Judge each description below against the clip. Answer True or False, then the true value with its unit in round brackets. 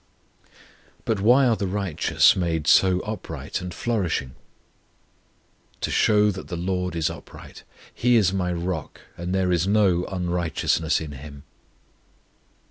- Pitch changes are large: False (3.0 semitones)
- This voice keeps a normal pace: False (130 wpm)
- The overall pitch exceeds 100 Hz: False (90 Hz)